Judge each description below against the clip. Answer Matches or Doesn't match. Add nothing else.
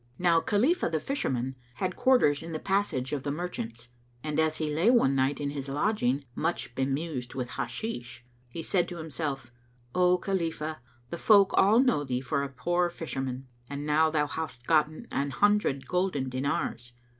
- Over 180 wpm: Doesn't match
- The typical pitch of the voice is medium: Matches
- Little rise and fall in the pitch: Doesn't match